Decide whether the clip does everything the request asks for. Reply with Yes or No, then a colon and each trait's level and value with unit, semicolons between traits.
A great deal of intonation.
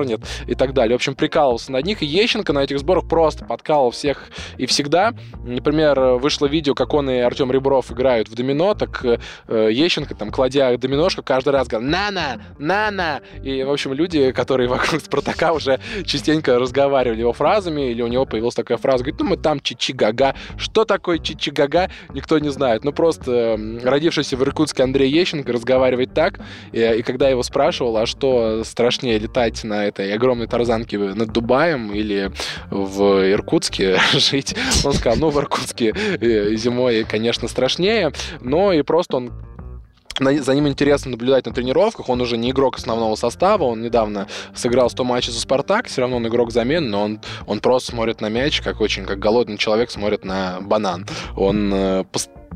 No: average, 3.9 semitones